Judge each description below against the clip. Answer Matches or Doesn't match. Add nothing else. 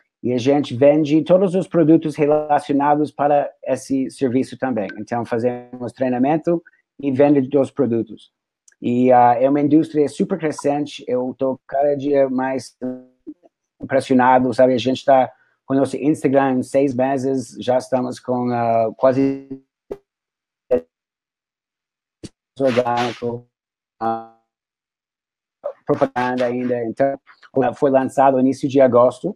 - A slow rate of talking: Matches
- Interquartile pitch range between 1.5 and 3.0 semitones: Matches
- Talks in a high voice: Doesn't match